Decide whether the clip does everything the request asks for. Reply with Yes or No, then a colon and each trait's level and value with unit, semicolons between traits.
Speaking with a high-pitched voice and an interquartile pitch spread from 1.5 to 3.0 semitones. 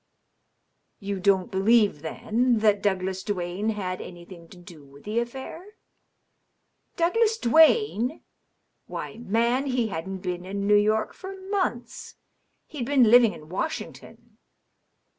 No: high, 210 Hz; average, 4.8 semitones